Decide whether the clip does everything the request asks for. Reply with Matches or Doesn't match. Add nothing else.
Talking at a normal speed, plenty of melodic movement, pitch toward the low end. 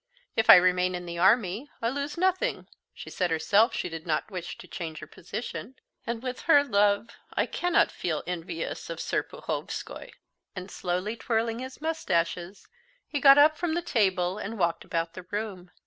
Doesn't match